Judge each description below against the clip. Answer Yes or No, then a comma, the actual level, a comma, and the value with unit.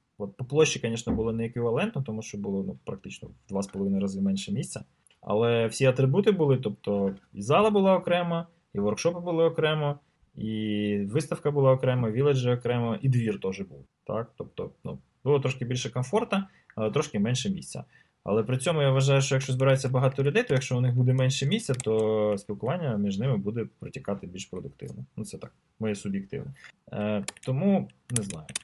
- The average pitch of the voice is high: No, low, 130 Hz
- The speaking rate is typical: No, fast, 175 wpm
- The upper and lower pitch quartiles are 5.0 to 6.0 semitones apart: Yes, average, 5.3 semitones